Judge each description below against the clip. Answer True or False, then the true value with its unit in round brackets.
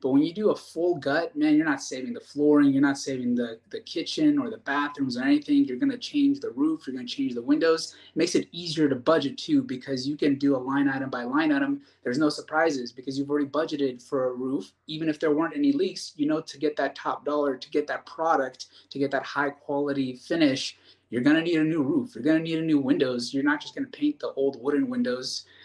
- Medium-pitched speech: True (150 Hz)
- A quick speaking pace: True (255 wpm)